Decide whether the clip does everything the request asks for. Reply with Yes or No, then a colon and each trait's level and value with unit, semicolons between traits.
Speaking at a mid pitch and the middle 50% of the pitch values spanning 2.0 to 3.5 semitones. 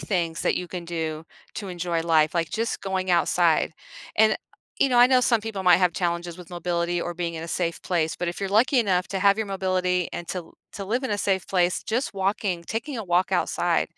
Yes: medium, 180 Hz; average, 2.8 semitones